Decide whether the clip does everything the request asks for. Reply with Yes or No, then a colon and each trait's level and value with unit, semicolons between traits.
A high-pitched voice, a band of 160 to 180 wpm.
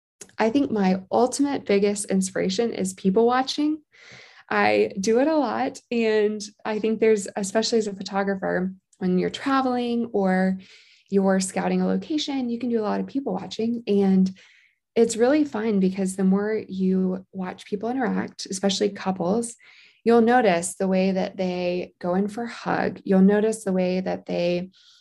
Yes: high, 200 Hz; average, 165 wpm